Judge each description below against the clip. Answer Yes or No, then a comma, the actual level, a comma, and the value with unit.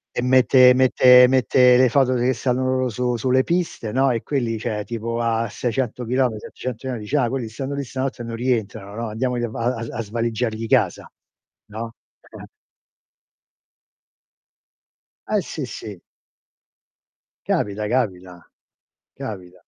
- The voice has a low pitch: Yes, low, 120 Hz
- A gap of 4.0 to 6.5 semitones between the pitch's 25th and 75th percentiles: No, narrow, 2.5 semitones